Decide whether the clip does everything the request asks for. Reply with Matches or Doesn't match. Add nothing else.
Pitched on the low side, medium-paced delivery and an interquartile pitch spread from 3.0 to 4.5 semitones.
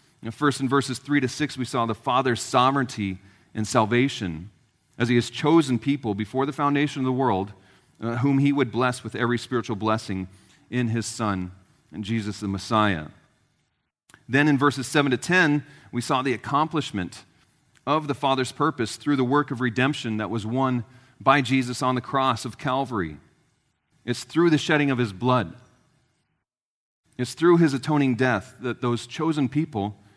Matches